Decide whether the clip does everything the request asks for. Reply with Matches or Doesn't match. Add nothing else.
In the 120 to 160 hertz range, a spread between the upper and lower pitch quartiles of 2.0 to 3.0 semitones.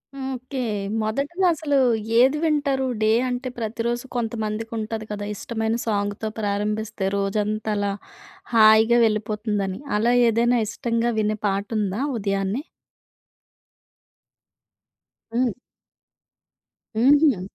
Doesn't match